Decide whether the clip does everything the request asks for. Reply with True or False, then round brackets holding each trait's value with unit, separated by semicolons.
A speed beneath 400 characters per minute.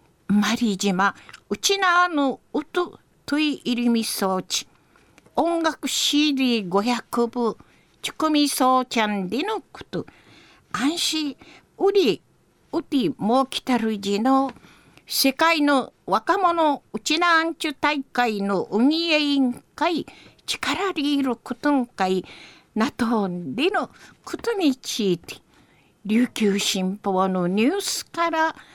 True (205 characters per minute)